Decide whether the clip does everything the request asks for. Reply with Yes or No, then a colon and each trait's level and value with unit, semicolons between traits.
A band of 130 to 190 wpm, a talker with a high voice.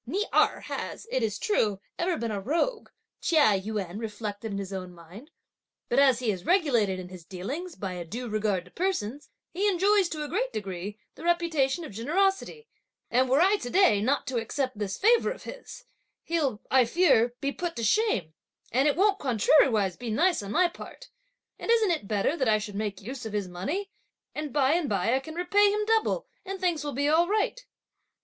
No: fast, 205 wpm; very high, 265 Hz